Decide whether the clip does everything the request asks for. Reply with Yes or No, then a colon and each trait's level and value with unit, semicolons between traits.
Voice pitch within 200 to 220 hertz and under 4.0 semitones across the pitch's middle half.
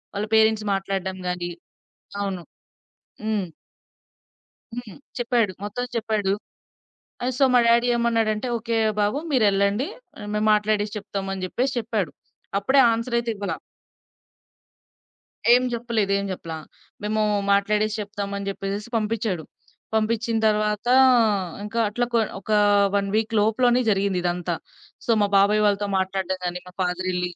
Yes: high, 210 Hz; average, 2.7 semitones